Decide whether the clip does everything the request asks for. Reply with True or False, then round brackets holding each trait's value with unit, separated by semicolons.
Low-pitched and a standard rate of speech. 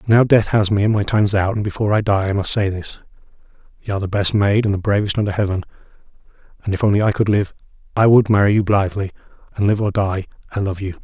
False (100 Hz; 245 wpm)